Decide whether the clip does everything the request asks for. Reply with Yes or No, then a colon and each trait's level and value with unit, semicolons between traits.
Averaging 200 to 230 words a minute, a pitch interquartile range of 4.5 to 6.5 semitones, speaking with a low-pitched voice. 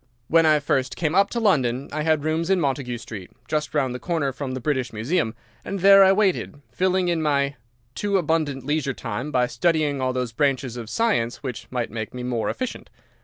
No: fast, 205 wpm; average, 4.9 semitones; medium, 145 Hz